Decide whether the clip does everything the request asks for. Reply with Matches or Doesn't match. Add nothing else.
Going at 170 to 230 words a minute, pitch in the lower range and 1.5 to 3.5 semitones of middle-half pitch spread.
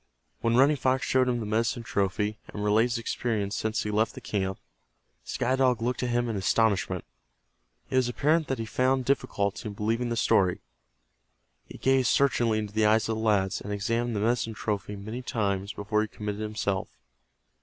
Matches